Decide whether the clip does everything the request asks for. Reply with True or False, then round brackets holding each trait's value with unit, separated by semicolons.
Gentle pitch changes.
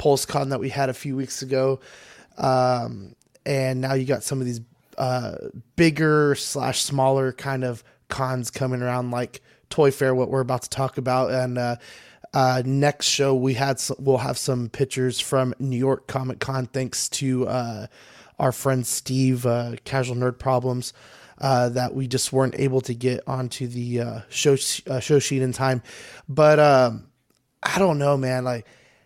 True (1.3 semitones)